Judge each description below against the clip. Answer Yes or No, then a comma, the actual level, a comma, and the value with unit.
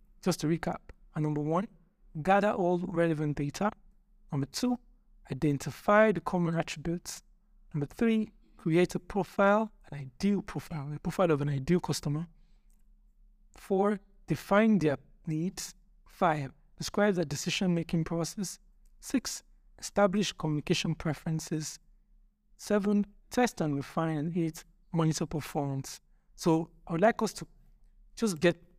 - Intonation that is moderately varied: Yes, average, 4.3 semitones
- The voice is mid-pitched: Yes, medium, 180 Hz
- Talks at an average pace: No, slow, 125 wpm